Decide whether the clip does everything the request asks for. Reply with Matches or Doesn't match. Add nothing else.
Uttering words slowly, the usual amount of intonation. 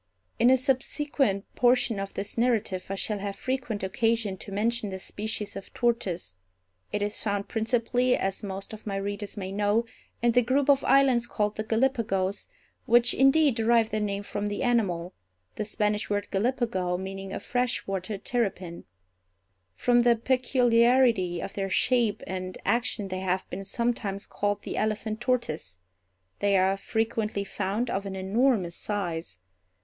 Doesn't match